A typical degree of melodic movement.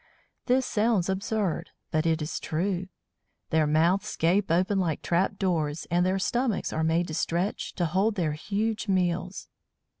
Yes: average, 3.4 semitones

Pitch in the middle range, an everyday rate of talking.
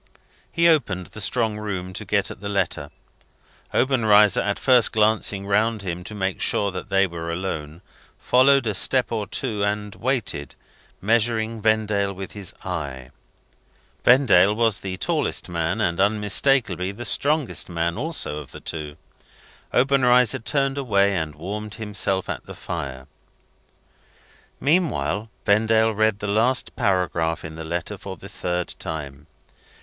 No: low, 100 Hz; average, 145 wpm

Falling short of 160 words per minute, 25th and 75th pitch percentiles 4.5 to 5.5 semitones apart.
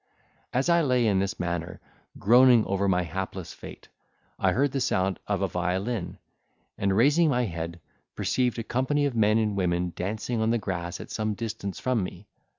No: average, 180 wpm; average, 5.2 semitones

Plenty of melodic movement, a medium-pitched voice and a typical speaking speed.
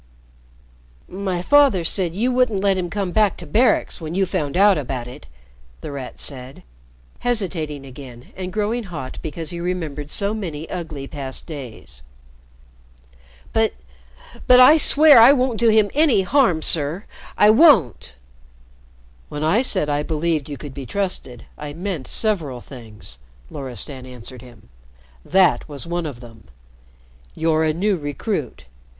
Yes: wide, 6.5 semitones; medium, 170 Hz; average, 145 wpm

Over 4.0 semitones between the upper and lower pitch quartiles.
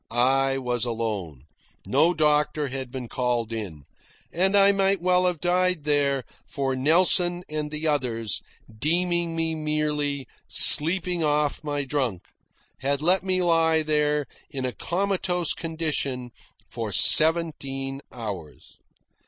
Yes: average, 4.6 semitones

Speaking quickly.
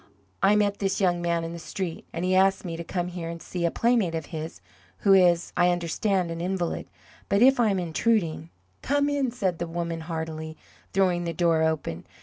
Yes: fast, 210 wpm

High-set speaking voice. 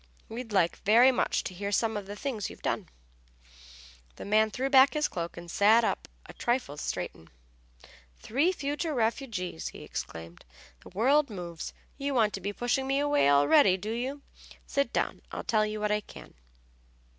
Yes: high, 220 Hz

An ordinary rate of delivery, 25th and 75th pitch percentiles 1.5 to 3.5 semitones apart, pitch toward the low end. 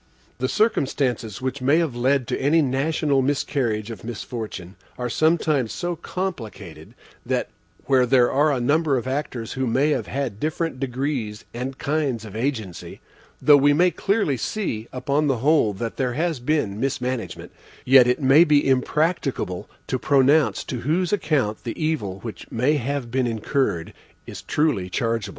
No: average, 160 wpm; average, 4.3 semitones; low, 130 Hz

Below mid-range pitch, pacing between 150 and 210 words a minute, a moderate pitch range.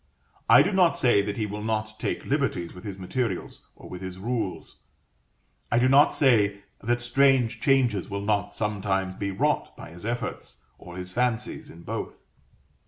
Yes: low, 105 Hz; average, 170 wpm; average, 4.1 semitones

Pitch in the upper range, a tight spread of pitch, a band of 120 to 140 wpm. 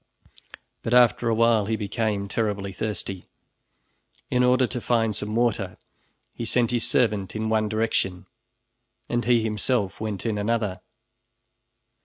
No: low, 110 Hz; narrow, 2.3 semitones; slow, 135 wpm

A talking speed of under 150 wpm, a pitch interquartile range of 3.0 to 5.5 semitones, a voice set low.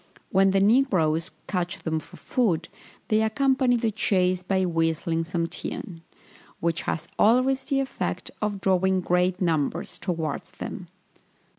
No: slow, 135 wpm; average, 4.5 semitones; medium, 185 Hz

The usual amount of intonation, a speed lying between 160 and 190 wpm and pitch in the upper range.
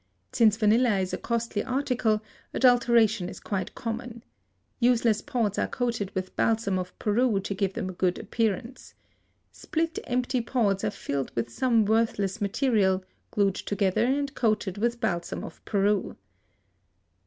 No: average, 3.5 semitones; average, 145 wpm; high, 220 Hz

